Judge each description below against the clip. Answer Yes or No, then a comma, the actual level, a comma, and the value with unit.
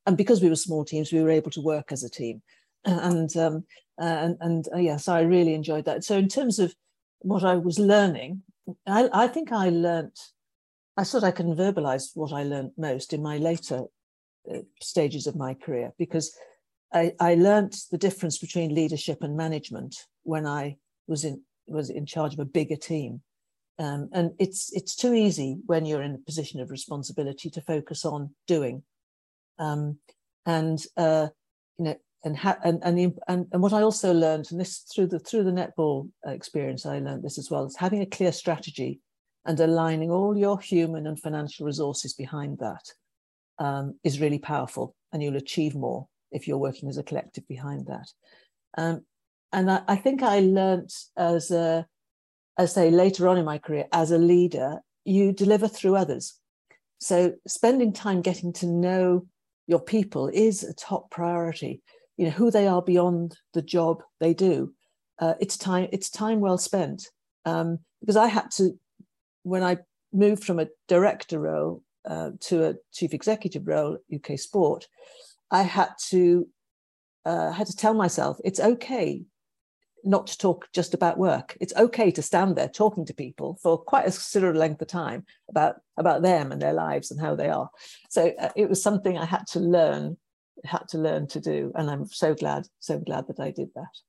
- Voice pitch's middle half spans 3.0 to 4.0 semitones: Yes, average, 3.6 semitones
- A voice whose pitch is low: No, medium, 170 Hz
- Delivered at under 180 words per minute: No, average, 185 wpm